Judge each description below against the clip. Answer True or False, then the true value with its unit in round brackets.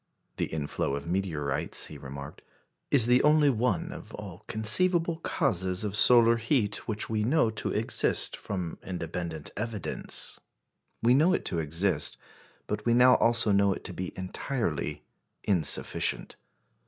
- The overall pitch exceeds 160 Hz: False (105 Hz)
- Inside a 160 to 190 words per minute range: False (140 wpm)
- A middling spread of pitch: False (5.9 semitones)